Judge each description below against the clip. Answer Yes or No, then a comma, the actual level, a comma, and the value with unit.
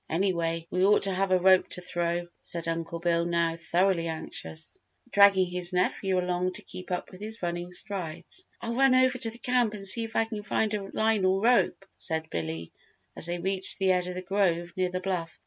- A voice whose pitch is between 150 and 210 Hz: Yes, medium, 185 Hz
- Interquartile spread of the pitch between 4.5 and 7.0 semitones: No, average, 2.7 semitones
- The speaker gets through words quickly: Yes, fast, 215 wpm